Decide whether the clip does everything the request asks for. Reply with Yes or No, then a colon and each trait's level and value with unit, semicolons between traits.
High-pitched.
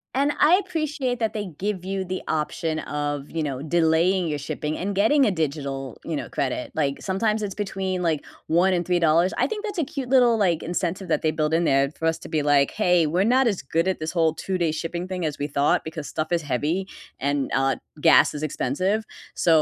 No: medium, 170 Hz